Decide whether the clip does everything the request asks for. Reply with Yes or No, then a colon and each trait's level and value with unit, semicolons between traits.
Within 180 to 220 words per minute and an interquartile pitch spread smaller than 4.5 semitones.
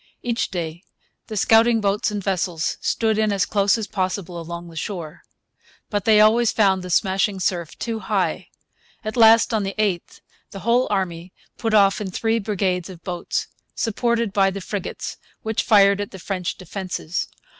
No: average, 170 wpm; average, 3.0 semitones